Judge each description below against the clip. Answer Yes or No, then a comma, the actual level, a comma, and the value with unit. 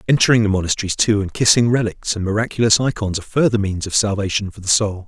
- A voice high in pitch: No, low, 105 Hz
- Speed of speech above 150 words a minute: Yes, average, 200 wpm